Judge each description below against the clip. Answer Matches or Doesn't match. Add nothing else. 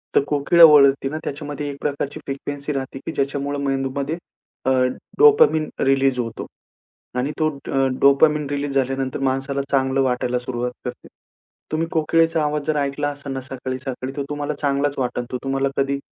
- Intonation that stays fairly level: Matches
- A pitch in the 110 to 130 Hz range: Doesn't match